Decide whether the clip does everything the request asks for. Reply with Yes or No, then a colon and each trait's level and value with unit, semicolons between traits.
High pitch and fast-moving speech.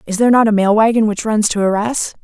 Yes: high, 215 Hz; fast, 270 wpm